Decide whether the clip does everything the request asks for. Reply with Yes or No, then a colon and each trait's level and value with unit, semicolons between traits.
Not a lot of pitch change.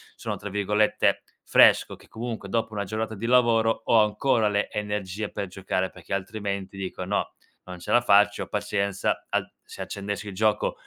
Yes: narrow, 1.9 semitones